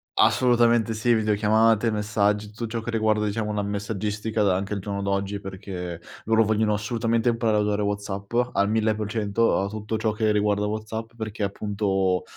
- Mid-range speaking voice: No, low, 105 Hz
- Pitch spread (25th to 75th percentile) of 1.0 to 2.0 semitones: Yes, narrow, 1.6 semitones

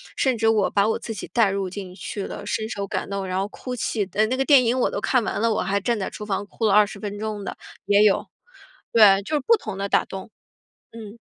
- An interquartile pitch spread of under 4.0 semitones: Yes, narrow, 2.4 semitones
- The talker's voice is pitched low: No, high, 210 Hz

